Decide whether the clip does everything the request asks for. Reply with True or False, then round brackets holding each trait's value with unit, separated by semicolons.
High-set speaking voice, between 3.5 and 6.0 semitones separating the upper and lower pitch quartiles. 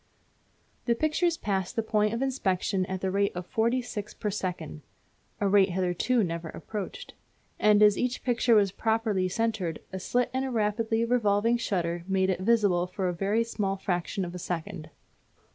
True (205 Hz; 3.8 semitones)